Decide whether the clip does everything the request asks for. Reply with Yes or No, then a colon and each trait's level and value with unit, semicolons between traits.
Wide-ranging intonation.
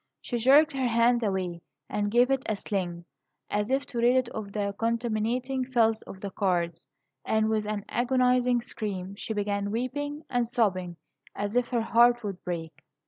No: average, 3.5 semitones